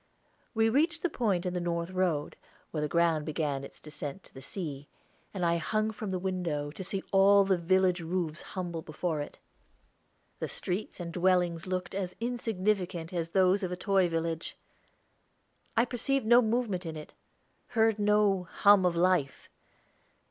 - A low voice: No, medium, 180 Hz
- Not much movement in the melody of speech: No, average, 3.3 semitones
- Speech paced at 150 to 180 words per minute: Yes, average, 165 wpm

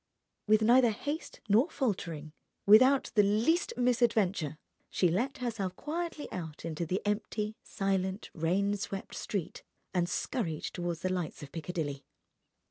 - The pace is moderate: No, slow, 130 wpm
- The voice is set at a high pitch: Yes, high, 200 Hz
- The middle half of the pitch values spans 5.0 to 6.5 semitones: Yes, wide, 5.5 semitones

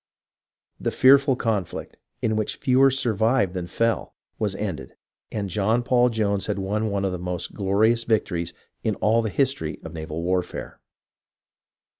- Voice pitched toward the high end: No, low, 105 Hz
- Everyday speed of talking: Yes, average, 155 wpm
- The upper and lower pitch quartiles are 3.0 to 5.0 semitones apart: Yes, average, 3.5 semitones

